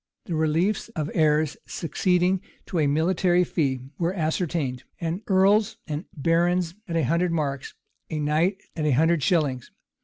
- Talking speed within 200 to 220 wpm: No, average, 150 wpm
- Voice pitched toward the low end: No, medium, 165 Hz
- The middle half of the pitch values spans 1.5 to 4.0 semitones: Yes, average, 2.9 semitones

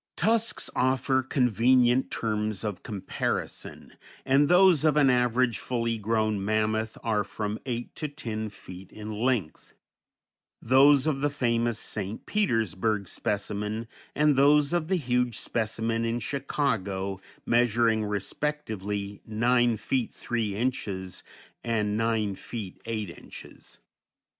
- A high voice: No, low, 115 Hz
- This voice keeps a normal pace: No, slow, 120 wpm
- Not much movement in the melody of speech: No, average, 3.6 semitones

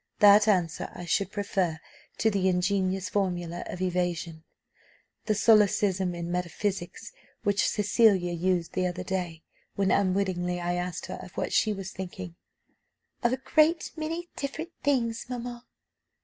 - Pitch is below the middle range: No, high, 190 Hz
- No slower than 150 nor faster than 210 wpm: No, average, 140 wpm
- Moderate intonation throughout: Yes, average, 3.2 semitones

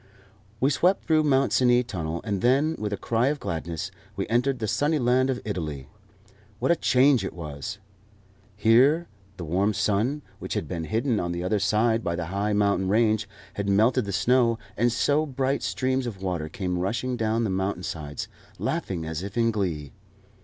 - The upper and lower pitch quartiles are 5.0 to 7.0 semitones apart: Yes, wide, 5.4 semitones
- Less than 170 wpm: No, average, 185 wpm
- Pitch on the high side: No, low, 110 Hz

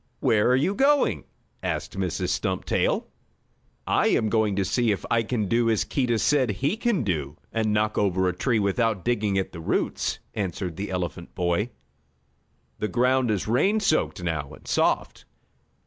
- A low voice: Yes, low, 110 Hz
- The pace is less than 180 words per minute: Yes, average, 165 wpm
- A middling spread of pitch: Yes, average, 4.8 semitones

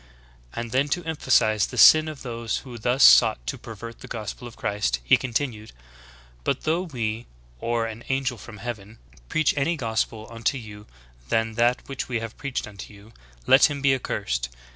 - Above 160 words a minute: Yes, average, 185 wpm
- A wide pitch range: No, average, 3.6 semitones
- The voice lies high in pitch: No, low, 115 Hz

